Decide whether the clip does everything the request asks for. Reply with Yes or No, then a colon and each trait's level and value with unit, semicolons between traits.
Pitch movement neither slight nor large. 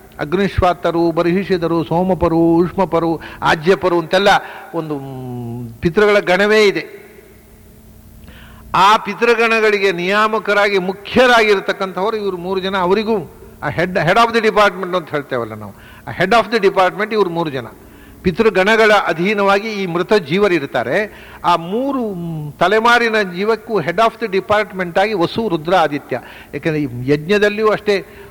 Yes: average, 3.9 semitones